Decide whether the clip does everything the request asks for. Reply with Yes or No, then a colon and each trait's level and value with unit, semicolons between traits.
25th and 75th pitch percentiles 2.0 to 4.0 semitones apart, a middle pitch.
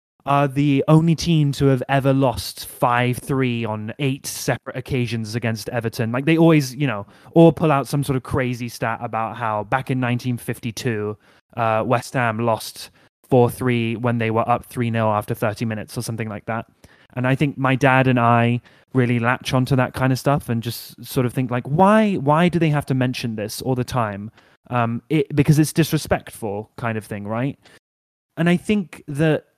No: average, 3.3 semitones; low, 125 Hz